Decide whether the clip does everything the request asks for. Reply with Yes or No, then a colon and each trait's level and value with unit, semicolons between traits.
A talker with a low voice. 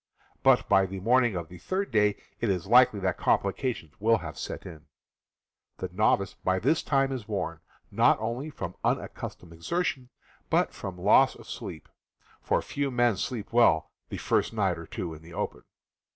Yes: low, 105 Hz